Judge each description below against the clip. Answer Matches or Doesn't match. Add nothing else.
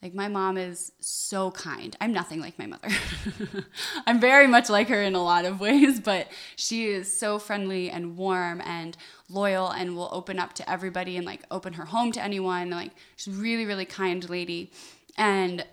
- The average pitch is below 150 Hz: Doesn't match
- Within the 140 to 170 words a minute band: Doesn't match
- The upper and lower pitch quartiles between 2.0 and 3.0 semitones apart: Matches